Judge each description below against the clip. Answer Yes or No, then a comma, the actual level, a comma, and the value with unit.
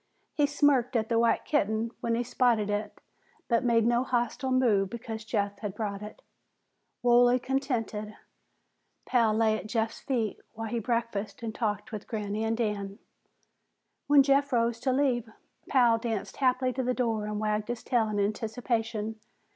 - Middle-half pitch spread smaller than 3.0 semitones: Yes, narrow, 2.5 semitones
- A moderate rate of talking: Yes, average, 165 wpm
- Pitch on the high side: Yes, high, 230 Hz